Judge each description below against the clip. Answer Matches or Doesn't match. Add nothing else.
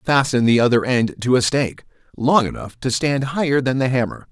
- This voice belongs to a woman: Doesn't match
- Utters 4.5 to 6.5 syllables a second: Matches